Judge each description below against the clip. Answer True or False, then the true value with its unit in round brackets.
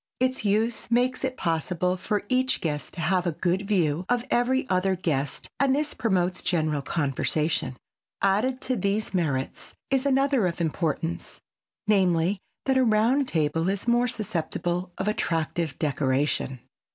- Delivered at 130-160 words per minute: True (145 wpm)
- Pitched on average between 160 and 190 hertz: True (185 Hz)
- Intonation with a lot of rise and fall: True (6.6 semitones)